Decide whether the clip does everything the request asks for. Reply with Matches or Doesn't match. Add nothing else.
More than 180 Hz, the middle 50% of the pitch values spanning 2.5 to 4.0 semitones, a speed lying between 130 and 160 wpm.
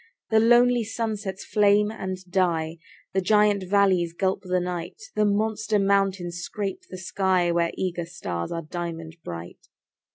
Matches